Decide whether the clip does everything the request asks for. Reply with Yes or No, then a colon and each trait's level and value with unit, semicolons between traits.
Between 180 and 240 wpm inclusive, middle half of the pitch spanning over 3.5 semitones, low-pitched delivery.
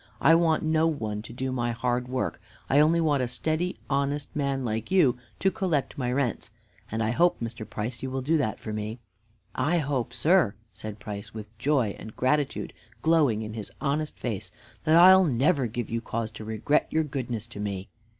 Yes: average, 195 wpm; average, 5.3 semitones; low, 130 Hz